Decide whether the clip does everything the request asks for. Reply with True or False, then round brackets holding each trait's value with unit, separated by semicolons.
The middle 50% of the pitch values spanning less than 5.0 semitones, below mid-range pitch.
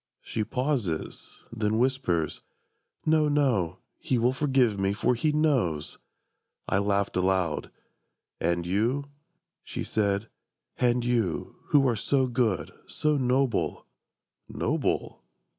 False (5.4 semitones; 120 Hz)